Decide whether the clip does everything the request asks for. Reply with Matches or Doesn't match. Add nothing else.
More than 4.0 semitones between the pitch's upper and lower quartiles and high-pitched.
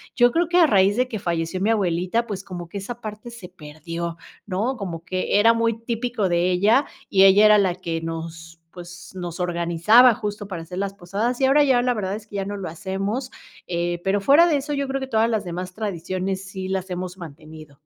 Matches